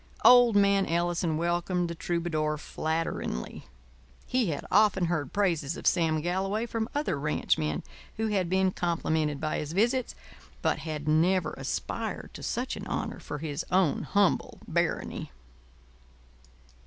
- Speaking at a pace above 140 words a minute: No, slow, 135 wpm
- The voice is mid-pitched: Yes, medium, 175 Hz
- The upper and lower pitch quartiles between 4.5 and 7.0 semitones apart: No, average, 3.9 semitones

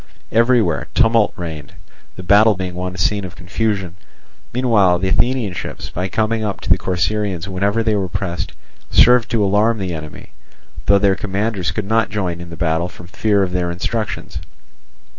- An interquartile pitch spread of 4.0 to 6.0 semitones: No, average, 3.4 semitones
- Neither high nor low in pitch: No, very low, 95 Hz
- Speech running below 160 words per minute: No, average, 170 wpm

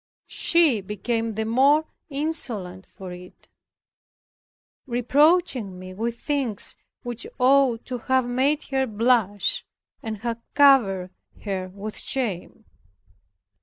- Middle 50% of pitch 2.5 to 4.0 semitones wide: No, average, 5.0 semitones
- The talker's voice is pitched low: No, high, 235 Hz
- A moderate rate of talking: No, slow, 105 wpm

